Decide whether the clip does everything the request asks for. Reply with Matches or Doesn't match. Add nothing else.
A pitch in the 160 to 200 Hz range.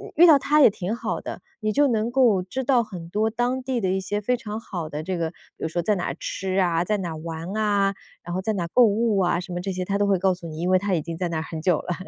Matches